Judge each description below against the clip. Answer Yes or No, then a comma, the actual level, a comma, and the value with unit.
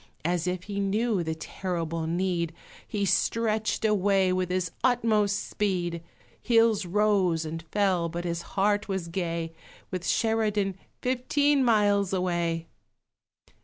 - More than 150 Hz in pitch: Yes, high, 190 Hz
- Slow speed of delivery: Yes, slow, 125 wpm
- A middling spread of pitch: Yes, average, 3.6 semitones